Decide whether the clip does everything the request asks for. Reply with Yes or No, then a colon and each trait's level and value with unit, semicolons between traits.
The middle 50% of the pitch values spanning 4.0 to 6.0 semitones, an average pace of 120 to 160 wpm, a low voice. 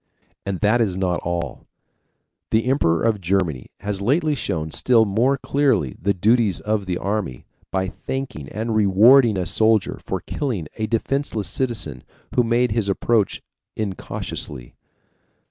Yes: average, 4.3 semitones; average, 140 wpm; low, 105 Hz